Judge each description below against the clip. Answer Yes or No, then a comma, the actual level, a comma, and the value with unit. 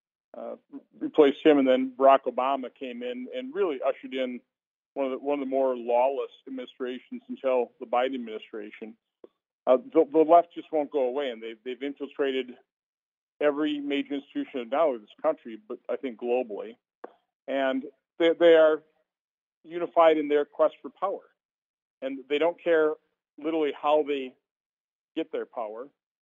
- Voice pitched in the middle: Yes, medium, 145 Hz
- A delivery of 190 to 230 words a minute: No, average, 160 wpm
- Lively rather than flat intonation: No, average, 3.6 semitones